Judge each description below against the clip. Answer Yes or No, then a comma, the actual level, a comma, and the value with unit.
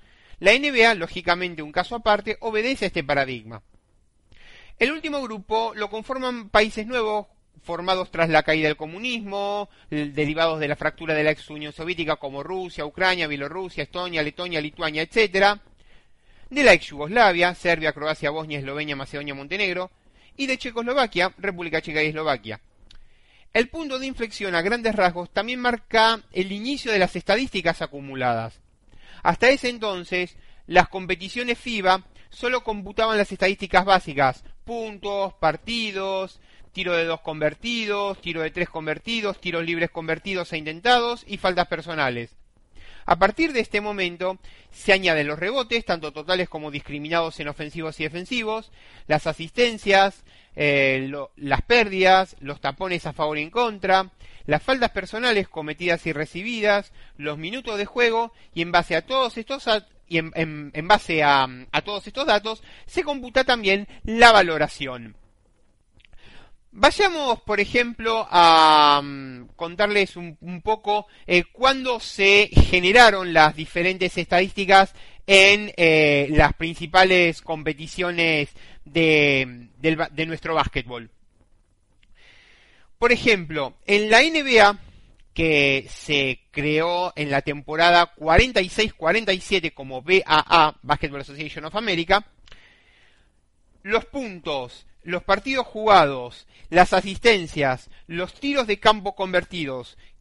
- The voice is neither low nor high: Yes, medium, 175 Hz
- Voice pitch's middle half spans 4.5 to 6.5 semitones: Yes, wide, 5.5 semitones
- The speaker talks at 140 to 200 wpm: No, slow, 125 wpm